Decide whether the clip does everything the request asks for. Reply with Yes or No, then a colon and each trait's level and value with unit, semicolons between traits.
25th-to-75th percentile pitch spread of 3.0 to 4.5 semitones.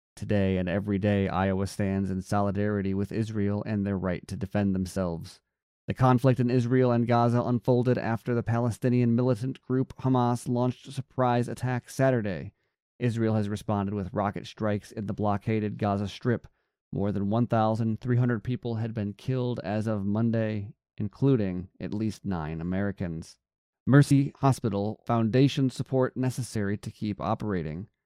Yes: average, 3.6 semitones